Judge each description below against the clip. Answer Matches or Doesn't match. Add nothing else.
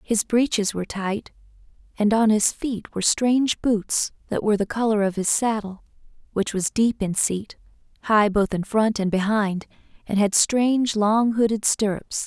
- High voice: Matches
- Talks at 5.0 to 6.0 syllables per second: Doesn't match